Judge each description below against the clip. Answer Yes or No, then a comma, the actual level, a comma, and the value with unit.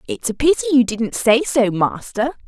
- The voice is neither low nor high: No, high, 245 Hz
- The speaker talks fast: No, average, 195 wpm